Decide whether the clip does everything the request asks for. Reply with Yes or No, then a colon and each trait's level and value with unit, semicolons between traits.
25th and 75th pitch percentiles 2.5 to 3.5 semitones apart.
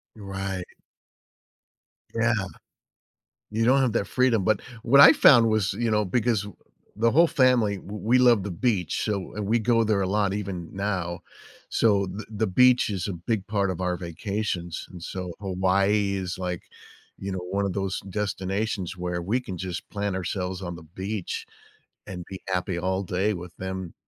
Yes: average, 2.8 semitones